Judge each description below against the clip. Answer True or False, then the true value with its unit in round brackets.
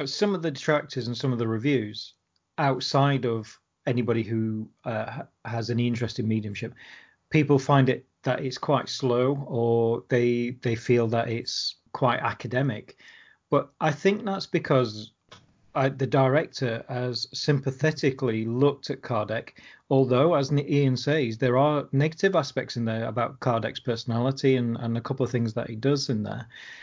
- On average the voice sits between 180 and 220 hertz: False (125 Hz)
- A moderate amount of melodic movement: True (3.3 semitones)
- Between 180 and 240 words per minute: False (160 wpm)